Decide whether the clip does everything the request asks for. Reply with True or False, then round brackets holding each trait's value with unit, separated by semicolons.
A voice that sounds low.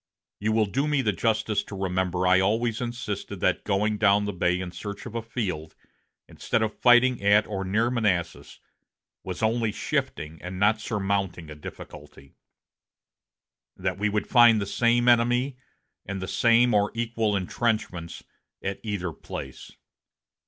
True (105 Hz)